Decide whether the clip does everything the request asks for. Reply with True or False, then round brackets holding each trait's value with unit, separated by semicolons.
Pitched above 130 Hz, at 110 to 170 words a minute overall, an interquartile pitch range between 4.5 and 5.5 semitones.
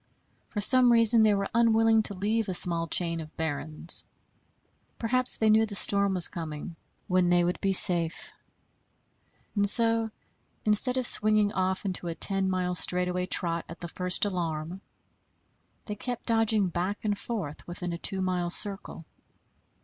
False (190 Hz; 155 wpm; 3.7 semitones)